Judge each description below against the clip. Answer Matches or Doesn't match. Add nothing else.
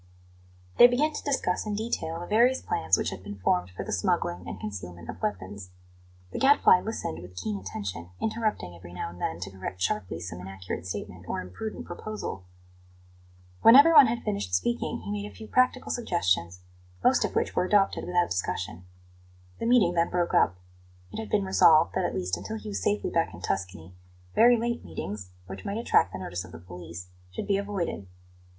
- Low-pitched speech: Matches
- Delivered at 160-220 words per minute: Matches